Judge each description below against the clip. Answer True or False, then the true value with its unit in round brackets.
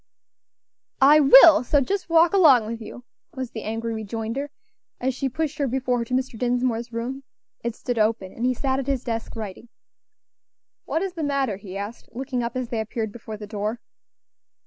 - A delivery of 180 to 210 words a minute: True (190 wpm)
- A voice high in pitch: True (245 Hz)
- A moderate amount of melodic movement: True (3.2 semitones)